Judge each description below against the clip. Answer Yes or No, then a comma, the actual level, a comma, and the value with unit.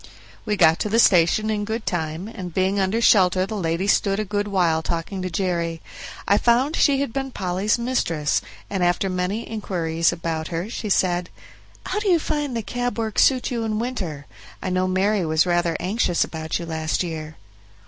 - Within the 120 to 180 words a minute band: No, average, 190 wpm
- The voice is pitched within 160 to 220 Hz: Yes, high, 190 Hz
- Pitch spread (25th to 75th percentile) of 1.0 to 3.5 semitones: No, average, 4.6 semitones